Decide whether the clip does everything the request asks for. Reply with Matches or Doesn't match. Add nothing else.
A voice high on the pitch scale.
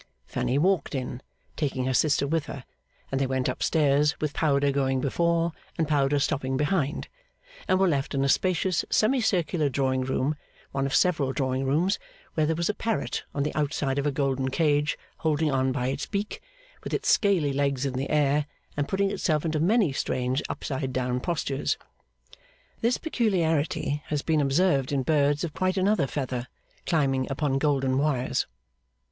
Doesn't match